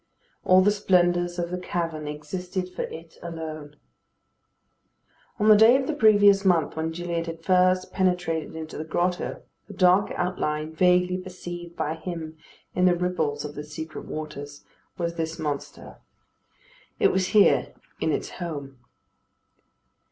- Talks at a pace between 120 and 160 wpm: Yes, average, 145 wpm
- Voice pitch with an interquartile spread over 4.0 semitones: No, narrow, 2.5 semitones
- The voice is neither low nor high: Yes, medium, 175 Hz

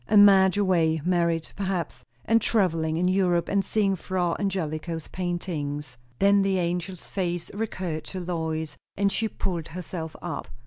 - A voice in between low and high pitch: Yes, medium, 180 Hz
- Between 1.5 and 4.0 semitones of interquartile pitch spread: Yes, average, 2.9 semitones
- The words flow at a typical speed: Yes, average, 145 wpm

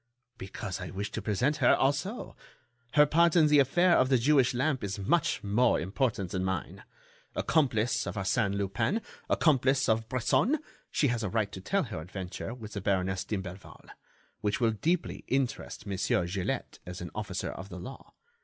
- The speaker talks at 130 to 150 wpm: No, average, 170 wpm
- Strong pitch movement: Yes, wide, 6.0 semitones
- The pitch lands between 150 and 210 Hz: No, low, 110 Hz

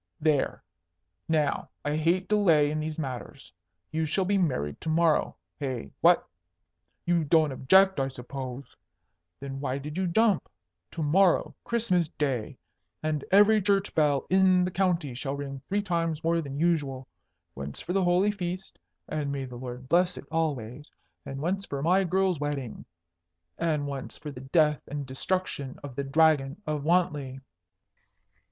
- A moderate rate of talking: Yes, average, 155 wpm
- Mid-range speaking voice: Yes, medium, 155 Hz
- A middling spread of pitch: Yes, average, 4.5 semitones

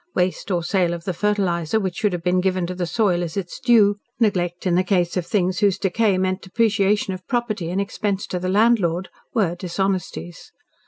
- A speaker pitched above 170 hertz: Yes, medium, 185 Hz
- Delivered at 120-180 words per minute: No, average, 200 wpm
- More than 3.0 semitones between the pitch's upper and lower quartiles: No, narrow, 2.6 semitones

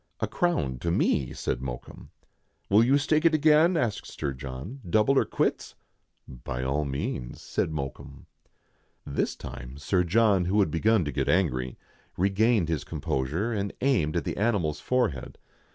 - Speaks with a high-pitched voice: No, very low, 85 Hz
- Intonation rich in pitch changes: Yes, wide, 8.9 semitones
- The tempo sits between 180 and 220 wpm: No, average, 165 wpm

